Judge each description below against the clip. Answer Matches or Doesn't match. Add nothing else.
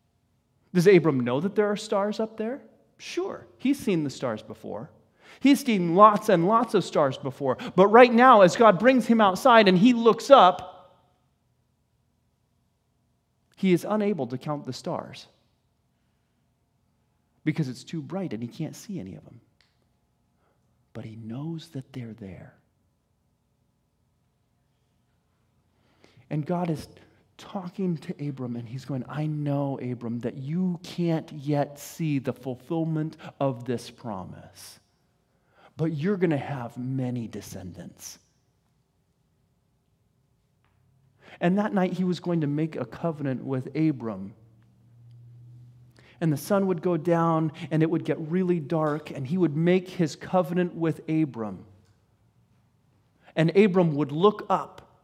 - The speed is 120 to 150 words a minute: Matches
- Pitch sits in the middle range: Matches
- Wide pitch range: Matches